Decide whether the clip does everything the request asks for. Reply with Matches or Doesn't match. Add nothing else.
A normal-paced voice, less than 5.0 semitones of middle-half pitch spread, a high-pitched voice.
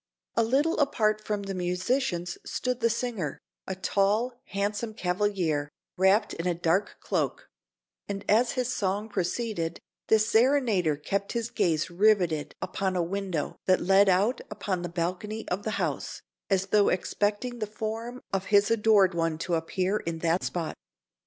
Matches